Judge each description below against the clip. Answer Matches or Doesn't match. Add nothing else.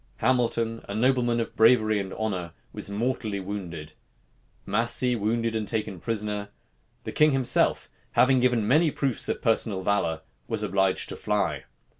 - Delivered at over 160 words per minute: Doesn't match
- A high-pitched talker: Doesn't match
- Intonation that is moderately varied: Matches